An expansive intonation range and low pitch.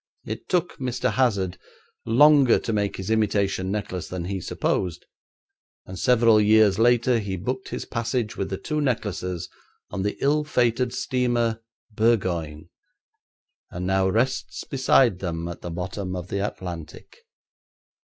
No: average, 4.7 semitones; low, 105 Hz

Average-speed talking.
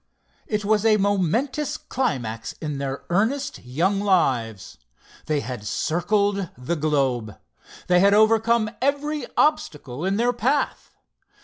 No: slow, 120 wpm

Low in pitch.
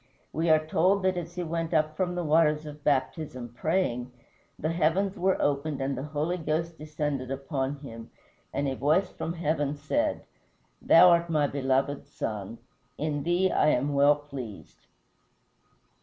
No: medium, 150 Hz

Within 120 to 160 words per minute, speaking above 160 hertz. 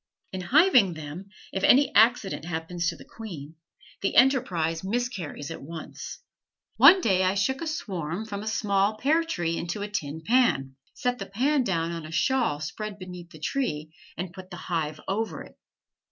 No: average, 175 wpm; high, 190 Hz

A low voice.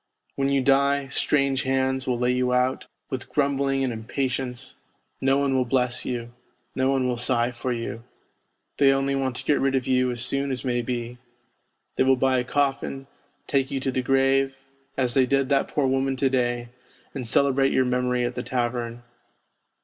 Yes: low, 130 Hz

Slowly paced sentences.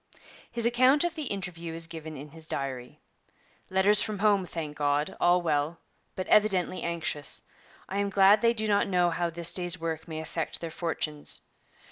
No: average, 175 wpm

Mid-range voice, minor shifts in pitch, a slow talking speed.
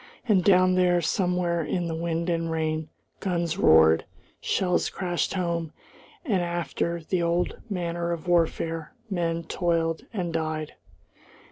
Yes: medium, 170 Hz; narrow, 1.5 semitones; slow, 130 wpm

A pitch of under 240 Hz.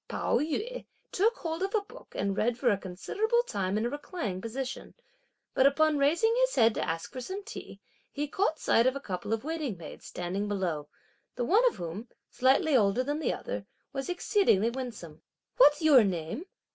No: very high, 260 Hz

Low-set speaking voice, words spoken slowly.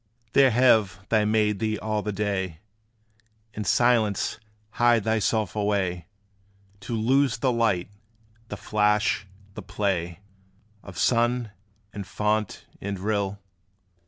Yes: low, 105 Hz; slow, 115 wpm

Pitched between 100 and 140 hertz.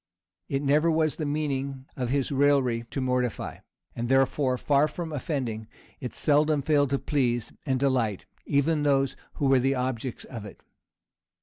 Yes: low, 135 Hz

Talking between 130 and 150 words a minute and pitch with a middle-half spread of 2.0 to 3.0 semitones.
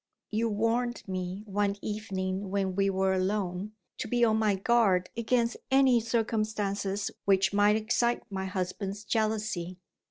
Yes: slow, 135 wpm; narrow, 2.6 semitones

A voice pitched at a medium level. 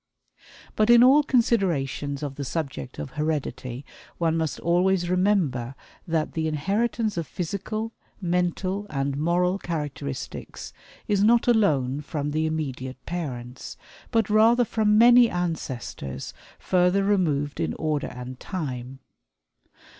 Yes: medium, 165 Hz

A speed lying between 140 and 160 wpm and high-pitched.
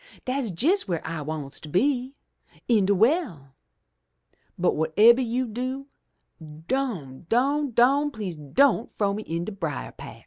Yes: average, 150 wpm; high, 220 Hz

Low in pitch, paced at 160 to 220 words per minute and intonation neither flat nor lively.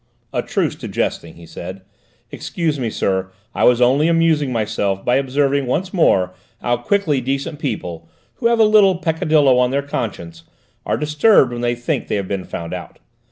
No: low, 130 Hz; average, 180 wpm; wide, 7.4 semitones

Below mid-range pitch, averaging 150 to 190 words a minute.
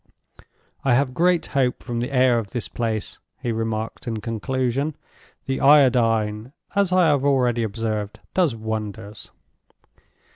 No: low, 120 Hz; slow, 135 wpm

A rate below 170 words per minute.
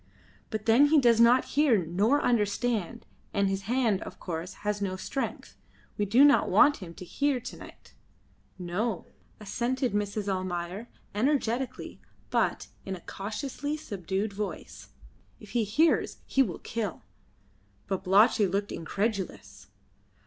Yes: slow, 135 wpm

